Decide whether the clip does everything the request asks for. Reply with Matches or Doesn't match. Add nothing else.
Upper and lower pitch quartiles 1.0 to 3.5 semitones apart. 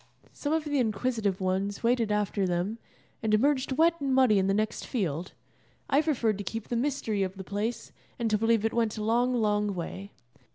Doesn't match